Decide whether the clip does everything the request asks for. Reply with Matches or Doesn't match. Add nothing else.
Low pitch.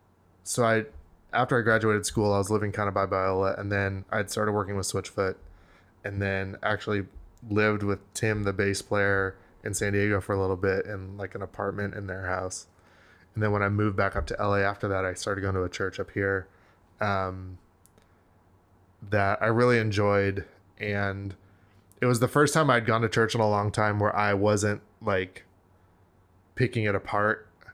Matches